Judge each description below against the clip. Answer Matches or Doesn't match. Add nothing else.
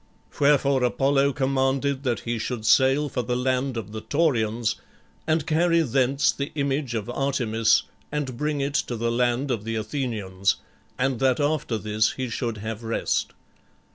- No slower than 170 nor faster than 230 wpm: Doesn't match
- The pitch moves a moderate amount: Matches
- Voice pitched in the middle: Doesn't match